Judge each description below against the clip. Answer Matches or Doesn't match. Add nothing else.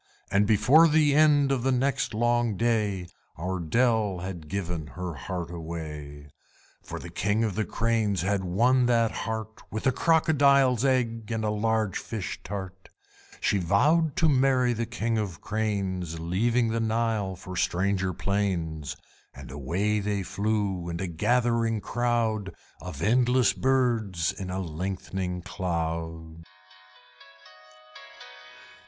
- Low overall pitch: Matches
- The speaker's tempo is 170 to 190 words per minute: Doesn't match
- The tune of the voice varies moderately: Matches